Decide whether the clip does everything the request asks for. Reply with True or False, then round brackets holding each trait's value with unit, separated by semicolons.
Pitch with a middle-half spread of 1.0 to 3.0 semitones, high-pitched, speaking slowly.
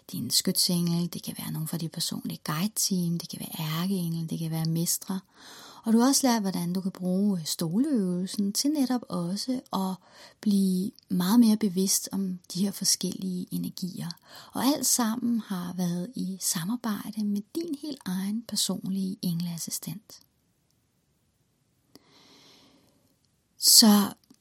False (3.7 semitones; 195 Hz; 140 wpm)